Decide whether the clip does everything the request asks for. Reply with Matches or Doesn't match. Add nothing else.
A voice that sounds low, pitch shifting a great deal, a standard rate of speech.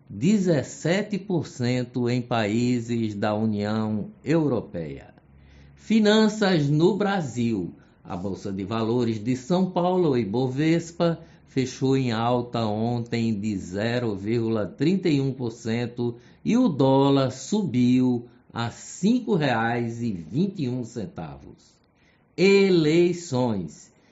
Doesn't match